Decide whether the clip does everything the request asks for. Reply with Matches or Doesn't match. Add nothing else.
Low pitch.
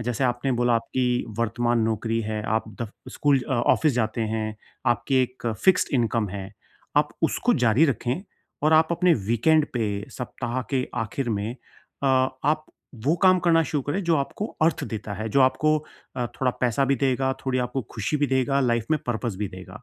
Matches